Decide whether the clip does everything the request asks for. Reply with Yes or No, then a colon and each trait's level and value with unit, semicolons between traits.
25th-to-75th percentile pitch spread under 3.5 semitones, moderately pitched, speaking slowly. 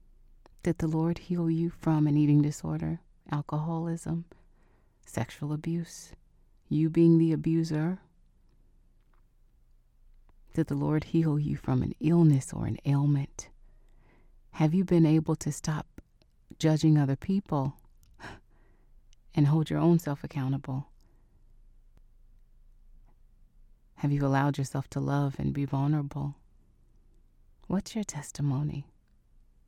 Yes: average, 3.0 semitones; medium, 150 Hz; slow, 110 wpm